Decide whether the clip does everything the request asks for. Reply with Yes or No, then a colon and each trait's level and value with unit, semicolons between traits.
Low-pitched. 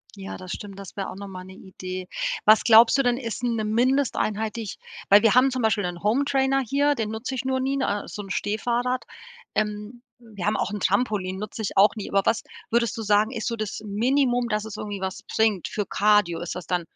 No: high, 215 Hz